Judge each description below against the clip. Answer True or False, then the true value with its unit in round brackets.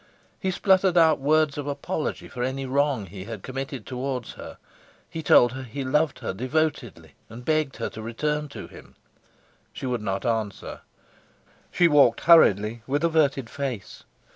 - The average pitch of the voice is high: False (135 Hz)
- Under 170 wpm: True (160 wpm)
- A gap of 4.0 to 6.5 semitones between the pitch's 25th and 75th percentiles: True (4.5 semitones)